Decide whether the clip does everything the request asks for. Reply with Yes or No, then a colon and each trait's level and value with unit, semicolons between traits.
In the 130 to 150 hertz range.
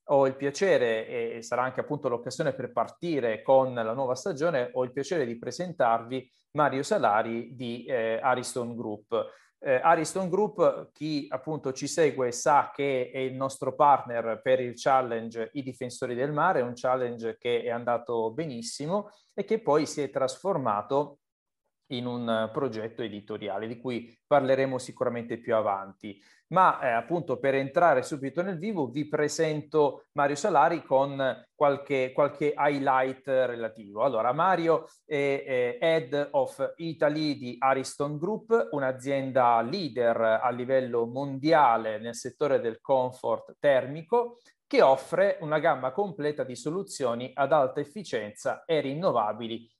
Yes: low, 135 Hz